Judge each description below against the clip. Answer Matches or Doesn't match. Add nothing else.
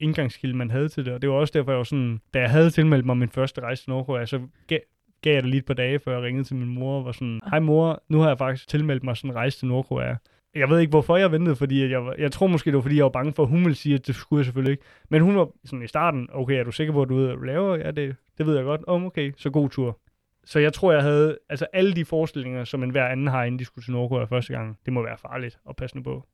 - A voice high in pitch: Doesn't match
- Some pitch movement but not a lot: Matches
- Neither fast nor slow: Doesn't match